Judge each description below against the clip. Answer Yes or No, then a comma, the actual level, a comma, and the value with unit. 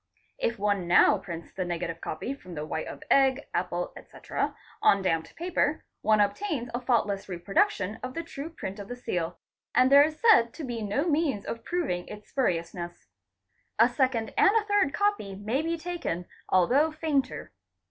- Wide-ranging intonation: Yes, wide, 8.4 semitones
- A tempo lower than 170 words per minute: No, average, 175 wpm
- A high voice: Yes, high, 230 Hz